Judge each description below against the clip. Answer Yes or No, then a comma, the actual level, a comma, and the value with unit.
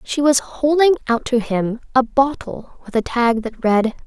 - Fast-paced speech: No, average, 190 wpm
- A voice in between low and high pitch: No, very high, 250 Hz